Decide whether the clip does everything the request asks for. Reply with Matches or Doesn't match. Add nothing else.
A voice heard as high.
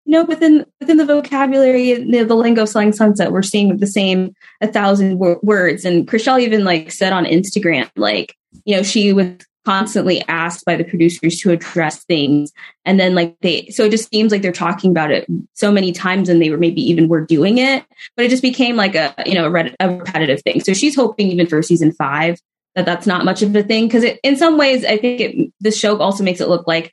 Matches